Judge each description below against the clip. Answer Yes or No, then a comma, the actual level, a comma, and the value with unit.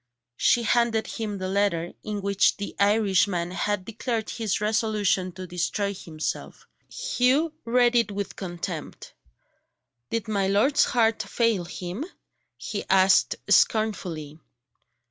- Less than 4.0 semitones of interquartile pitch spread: Yes, average, 3.2 semitones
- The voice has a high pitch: Yes, high, 205 Hz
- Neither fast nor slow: No, slow, 120 wpm